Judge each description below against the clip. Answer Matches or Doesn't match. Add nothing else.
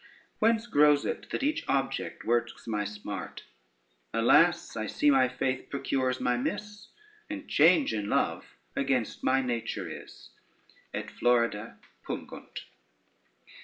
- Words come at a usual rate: Doesn't match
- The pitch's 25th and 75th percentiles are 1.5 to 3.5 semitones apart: Doesn't match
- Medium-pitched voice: Doesn't match